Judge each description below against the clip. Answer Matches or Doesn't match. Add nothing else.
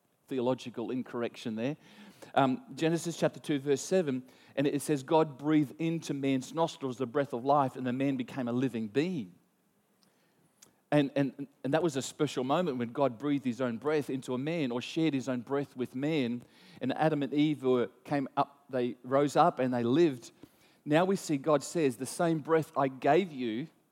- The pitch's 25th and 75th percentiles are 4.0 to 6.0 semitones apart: Doesn't match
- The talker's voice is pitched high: Doesn't match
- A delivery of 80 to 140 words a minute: Doesn't match